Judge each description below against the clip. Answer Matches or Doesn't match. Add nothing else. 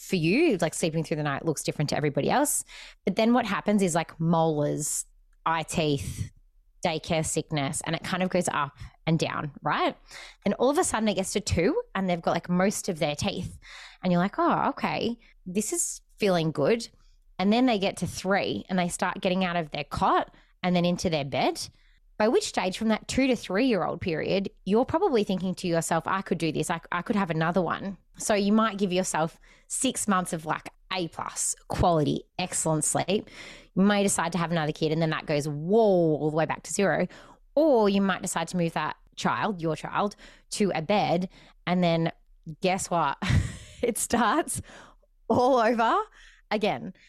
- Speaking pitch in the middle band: Matches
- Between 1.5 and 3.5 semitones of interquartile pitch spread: Doesn't match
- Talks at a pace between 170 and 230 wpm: Matches